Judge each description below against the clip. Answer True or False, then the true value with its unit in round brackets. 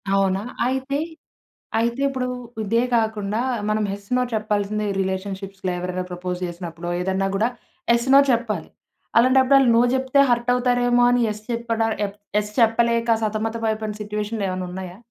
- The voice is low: False (215 Hz)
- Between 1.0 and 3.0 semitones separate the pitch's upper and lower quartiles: False (3.5 semitones)